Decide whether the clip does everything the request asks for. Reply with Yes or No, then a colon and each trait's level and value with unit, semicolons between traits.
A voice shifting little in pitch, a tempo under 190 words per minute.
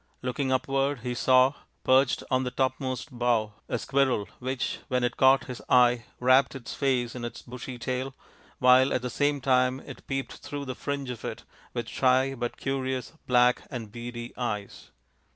Yes: narrow, 1.5 semitones; average, 170 wpm